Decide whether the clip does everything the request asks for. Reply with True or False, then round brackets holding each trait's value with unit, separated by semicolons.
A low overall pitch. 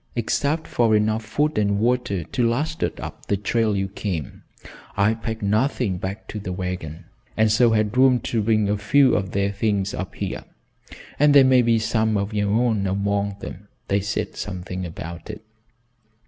True (105 Hz)